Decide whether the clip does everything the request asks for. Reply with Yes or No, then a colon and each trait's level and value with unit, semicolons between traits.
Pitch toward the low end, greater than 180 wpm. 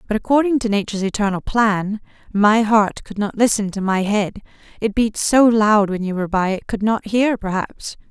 No: high, 210 Hz; average, 190 wpm